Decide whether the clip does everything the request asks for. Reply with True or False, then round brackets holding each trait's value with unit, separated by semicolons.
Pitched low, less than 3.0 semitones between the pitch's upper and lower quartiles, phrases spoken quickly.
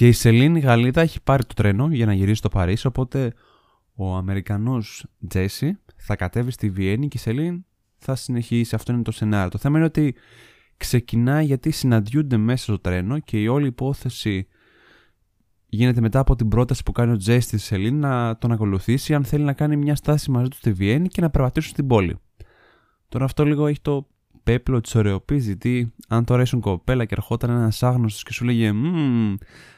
False (120 Hz; 4.2 semitones; 185 wpm)